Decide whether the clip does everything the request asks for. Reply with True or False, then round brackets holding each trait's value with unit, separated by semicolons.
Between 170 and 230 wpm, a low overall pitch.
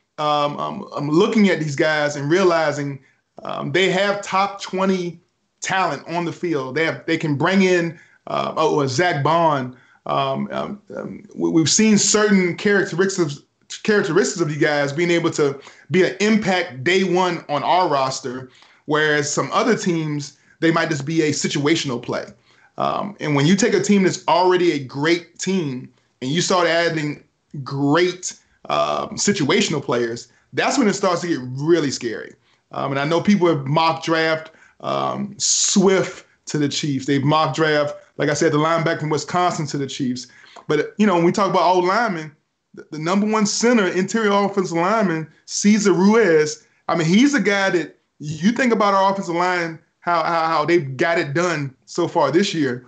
False (180 wpm; 165 Hz)